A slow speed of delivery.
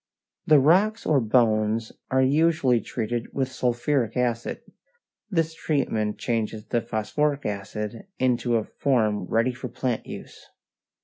Yes: slow, 125 wpm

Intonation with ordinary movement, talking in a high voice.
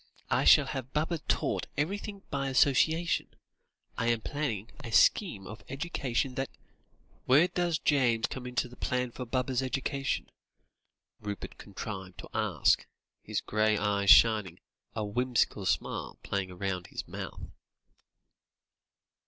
No: average, 4.6 semitones; low, 125 Hz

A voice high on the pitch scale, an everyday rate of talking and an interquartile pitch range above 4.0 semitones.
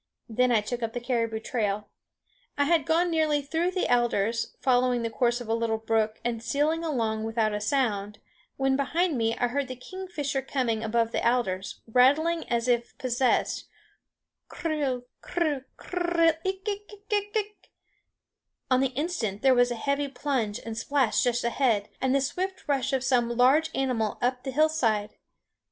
Yes: very high, 255 Hz; average, 165 wpm; average, 4.5 semitones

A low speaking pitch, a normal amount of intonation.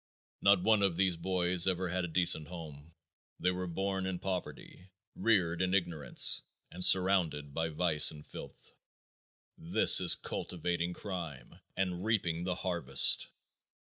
No: very low, 90 Hz; narrow, 2.1 semitones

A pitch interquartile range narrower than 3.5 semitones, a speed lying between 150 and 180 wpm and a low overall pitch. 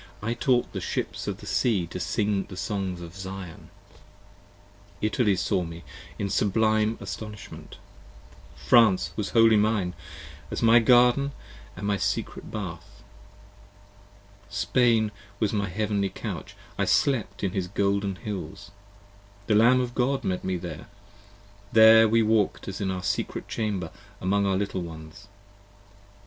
No: average, 3.0 semitones; average, 140 wpm; low, 100 Hz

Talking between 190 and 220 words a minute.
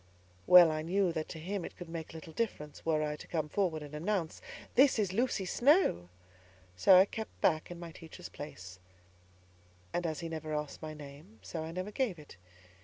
Yes: average, 195 wpm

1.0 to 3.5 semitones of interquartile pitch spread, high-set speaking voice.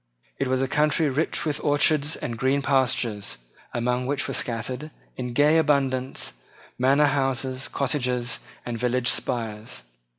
No: narrow, 2.5 semitones; low, 130 Hz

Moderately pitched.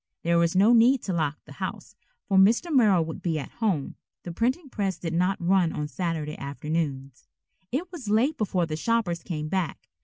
Yes: medium, 180 Hz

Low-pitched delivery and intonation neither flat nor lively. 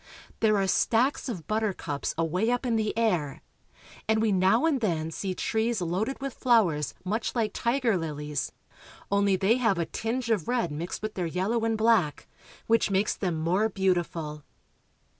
No: high, 205 Hz; average, 4.8 semitones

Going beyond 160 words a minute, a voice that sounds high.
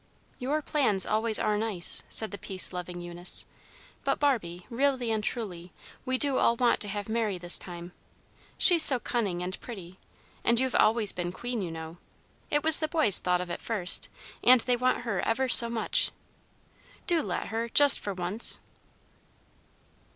Yes: average, 170 wpm; high, 220 Hz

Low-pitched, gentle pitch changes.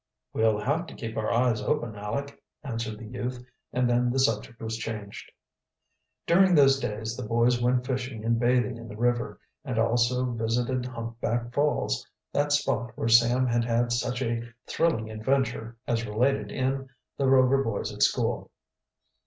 Yes: low, 120 Hz; narrow, 2.3 semitones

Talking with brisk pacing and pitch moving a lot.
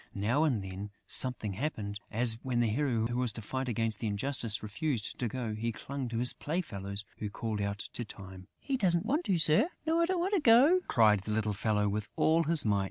Yes: fast, 220 wpm; wide, 6.5 semitones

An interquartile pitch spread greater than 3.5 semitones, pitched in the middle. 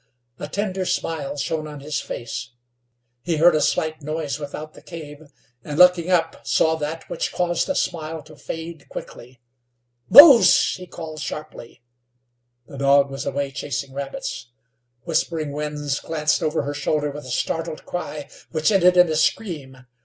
No: narrow, 2.5 semitones; medium, 155 Hz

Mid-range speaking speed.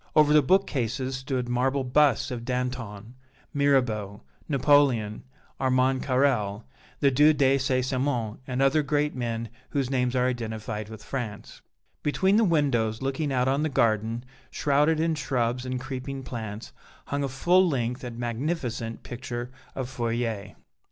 Yes: average, 145 wpm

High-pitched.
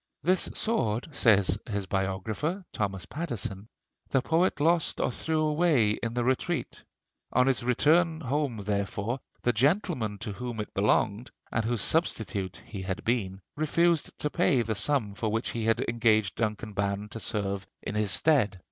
No: low, 115 Hz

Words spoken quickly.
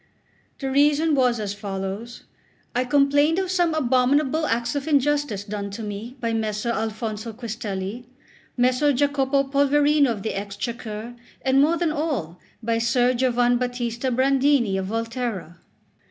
No: slow, 135 wpm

